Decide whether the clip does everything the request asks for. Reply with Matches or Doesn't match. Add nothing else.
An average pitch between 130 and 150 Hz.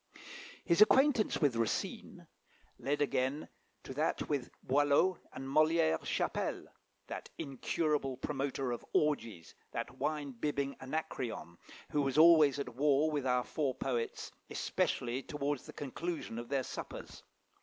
Matches